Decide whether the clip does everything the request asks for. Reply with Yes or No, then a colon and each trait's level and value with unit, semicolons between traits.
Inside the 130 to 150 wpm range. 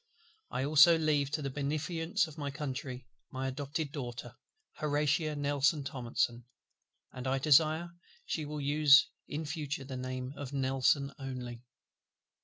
Yes: slow, 135 wpm